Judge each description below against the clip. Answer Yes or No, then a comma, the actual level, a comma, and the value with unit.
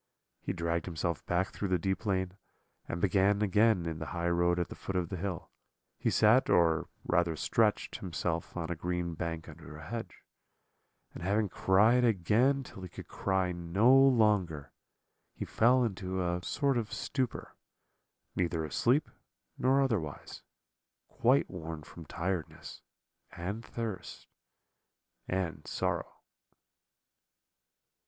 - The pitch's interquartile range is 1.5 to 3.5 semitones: No, average, 4.2 semitones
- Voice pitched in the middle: No, very low, 90 Hz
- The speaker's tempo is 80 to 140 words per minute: Yes, slow, 135 wpm